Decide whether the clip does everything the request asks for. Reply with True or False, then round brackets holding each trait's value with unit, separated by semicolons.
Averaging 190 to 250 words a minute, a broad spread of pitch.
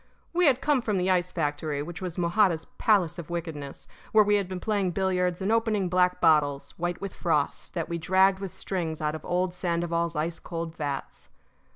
False (195 wpm; 2.7 semitones)